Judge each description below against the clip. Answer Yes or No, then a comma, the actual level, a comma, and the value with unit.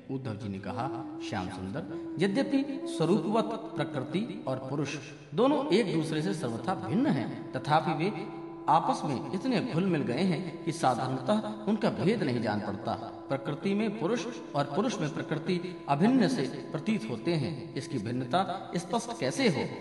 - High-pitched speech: No, medium, 165 Hz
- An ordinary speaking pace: Yes, average, 155 wpm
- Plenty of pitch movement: Yes, wide, 5.7 semitones